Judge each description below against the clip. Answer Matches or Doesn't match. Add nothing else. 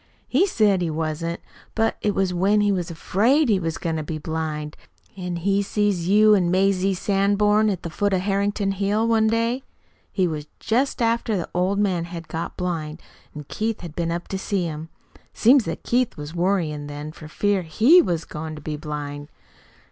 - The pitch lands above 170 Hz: Matches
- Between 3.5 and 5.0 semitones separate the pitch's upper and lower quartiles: Matches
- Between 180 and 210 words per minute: Matches